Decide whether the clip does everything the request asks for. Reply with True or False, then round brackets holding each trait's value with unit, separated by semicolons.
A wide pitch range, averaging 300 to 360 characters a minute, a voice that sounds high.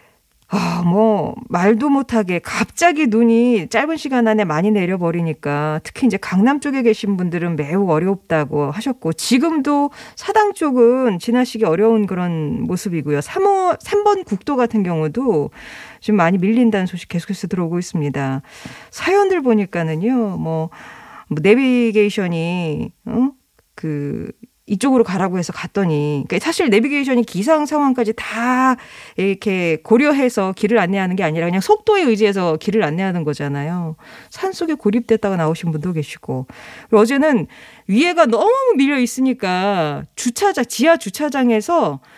True (6.5 semitones; 320 characters per minute; 215 Hz)